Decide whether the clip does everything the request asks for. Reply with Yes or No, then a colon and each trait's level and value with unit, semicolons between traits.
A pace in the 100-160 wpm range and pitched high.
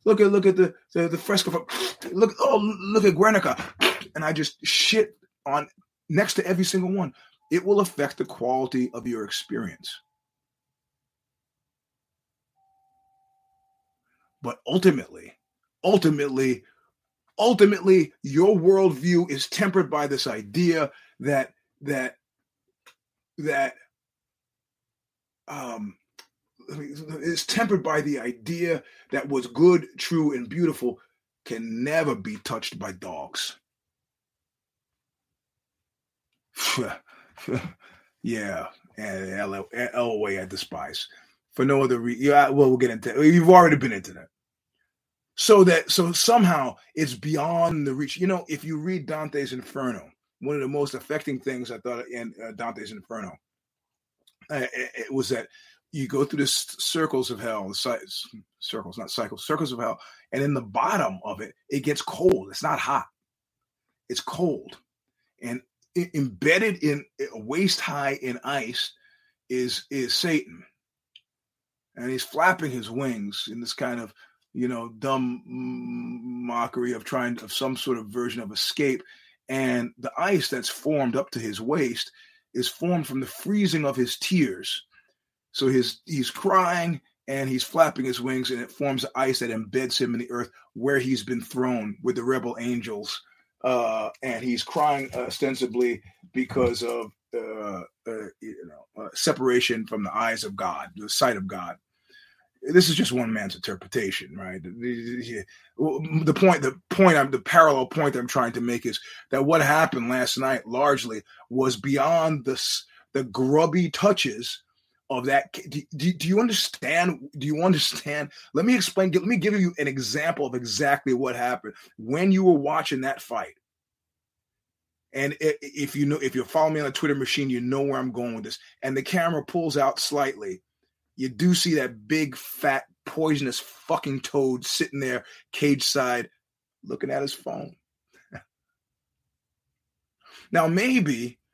No: average, 150 wpm; medium, 140 Hz